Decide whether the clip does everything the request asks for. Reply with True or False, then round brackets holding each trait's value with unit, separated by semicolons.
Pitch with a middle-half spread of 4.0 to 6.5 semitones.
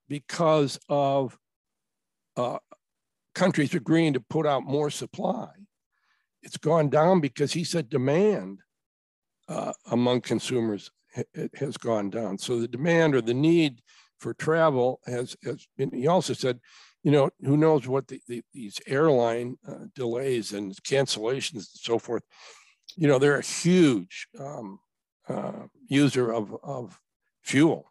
True (4.7 semitones)